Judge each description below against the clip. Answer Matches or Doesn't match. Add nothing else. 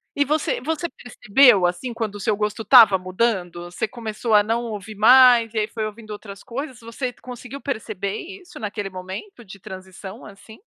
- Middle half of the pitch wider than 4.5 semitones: Doesn't match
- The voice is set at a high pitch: Matches